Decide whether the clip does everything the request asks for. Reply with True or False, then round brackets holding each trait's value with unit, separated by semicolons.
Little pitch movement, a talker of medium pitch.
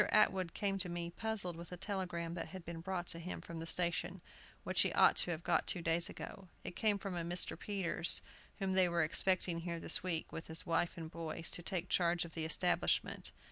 True (2.0 semitones; 175 Hz)